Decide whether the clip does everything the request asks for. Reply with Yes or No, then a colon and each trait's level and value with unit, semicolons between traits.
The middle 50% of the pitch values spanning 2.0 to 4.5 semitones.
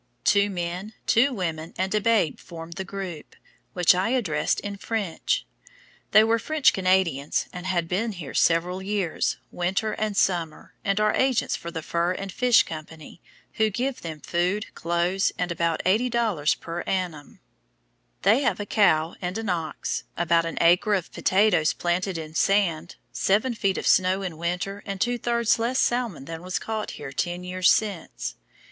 Yes: average, 3.9 semitones